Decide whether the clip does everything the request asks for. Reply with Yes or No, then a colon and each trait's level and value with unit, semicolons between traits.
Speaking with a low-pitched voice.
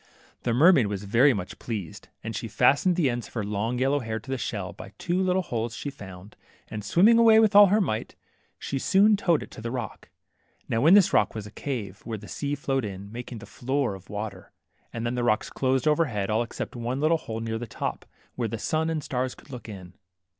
Yes: low, 120 Hz